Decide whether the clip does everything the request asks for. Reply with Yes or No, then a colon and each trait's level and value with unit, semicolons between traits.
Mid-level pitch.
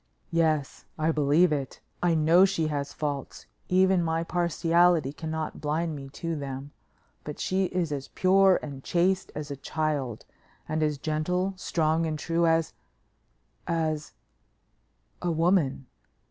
Yes: medium, 160 Hz